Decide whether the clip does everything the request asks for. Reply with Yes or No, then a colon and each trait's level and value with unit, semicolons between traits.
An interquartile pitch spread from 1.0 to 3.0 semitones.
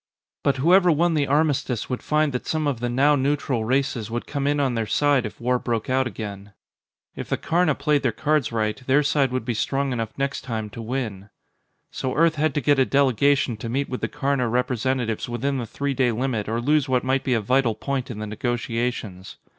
No: average, 3.4 semitones